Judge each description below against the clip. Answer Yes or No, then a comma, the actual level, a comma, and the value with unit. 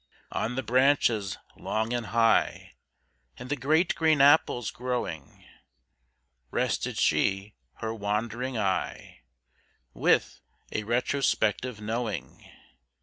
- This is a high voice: No, low, 115 Hz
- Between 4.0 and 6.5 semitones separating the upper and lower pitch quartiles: No, average, 3.3 semitones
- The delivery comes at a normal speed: No, slow, 95 wpm